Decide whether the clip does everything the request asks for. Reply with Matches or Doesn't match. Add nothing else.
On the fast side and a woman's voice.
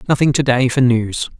Doesn't match